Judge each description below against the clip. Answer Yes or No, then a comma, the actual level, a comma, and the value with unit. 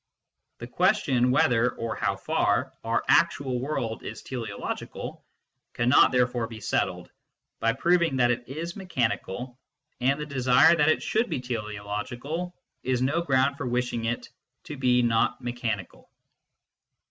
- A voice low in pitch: Yes, low, 125 Hz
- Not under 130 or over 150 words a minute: Yes, average, 140 wpm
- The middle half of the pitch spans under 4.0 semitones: Yes, average, 3.0 semitones